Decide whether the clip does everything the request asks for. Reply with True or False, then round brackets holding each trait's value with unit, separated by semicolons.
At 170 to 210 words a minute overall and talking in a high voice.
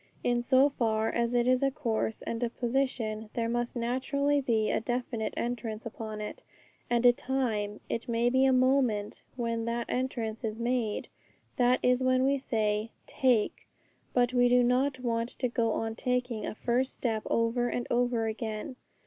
True (175 wpm; 240 Hz)